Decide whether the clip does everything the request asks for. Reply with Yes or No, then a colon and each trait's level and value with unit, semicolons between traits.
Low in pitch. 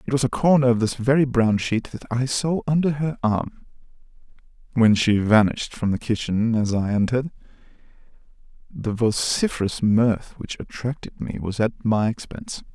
Yes: low, 120 Hz